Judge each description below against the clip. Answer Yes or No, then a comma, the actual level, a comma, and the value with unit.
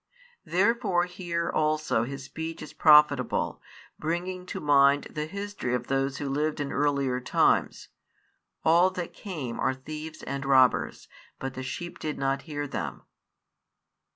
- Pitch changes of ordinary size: Yes, average, 3.9 semitones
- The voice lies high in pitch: No, medium, 150 Hz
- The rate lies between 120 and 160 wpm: Yes, average, 140 wpm